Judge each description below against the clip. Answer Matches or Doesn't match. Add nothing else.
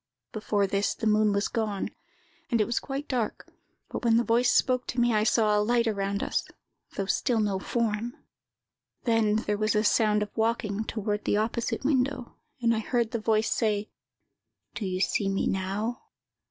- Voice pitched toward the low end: Doesn't match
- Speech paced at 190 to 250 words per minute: Doesn't match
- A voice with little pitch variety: Matches